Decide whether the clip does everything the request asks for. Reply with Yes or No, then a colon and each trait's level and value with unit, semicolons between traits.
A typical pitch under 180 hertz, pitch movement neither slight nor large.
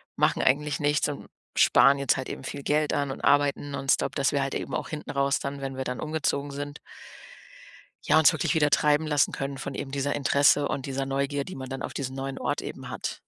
No: medium, 140 Hz; narrow, 1.2 semitones